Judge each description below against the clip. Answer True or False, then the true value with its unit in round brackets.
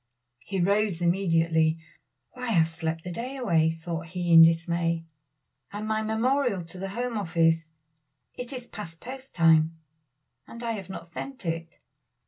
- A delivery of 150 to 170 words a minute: True (155 wpm)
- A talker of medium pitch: True (175 Hz)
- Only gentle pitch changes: False (5.0 semitones)